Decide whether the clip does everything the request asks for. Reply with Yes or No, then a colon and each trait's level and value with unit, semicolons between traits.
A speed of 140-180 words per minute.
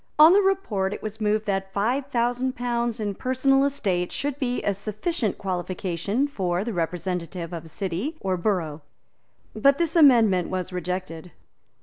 Yes: average, 155 wpm